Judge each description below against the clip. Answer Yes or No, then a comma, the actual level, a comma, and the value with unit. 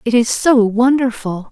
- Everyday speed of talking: Yes, average, 160 wpm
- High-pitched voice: Yes, high, 235 Hz